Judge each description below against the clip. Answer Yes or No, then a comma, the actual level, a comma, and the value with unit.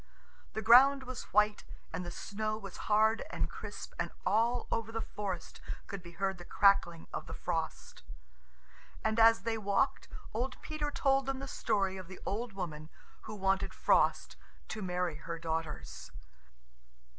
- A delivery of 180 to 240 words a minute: No, average, 155 wpm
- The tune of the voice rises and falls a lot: No, average, 4.1 semitones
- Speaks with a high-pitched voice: Yes, high, 210 Hz